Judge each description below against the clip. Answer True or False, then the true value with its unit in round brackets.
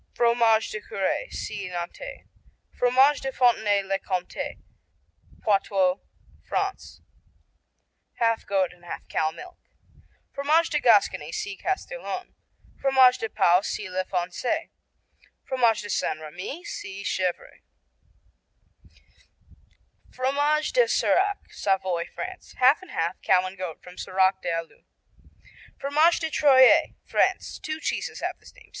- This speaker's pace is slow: True (125 wpm)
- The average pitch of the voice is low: False (220 Hz)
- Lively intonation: True (7.6 semitones)